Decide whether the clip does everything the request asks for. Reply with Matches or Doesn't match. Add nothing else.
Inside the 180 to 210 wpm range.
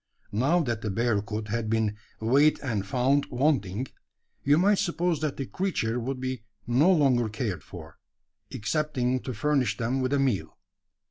Doesn't match